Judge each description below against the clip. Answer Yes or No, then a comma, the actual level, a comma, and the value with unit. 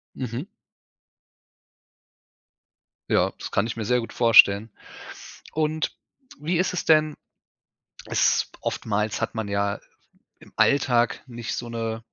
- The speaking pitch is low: Yes, low, 115 Hz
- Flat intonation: No, average, 5.3 semitones